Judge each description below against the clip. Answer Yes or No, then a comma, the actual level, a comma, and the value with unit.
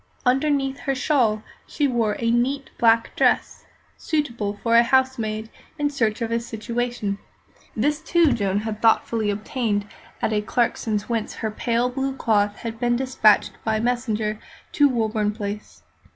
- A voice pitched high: Yes, high, 230 Hz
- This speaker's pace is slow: No, average, 145 wpm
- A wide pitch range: No, average, 3.4 semitones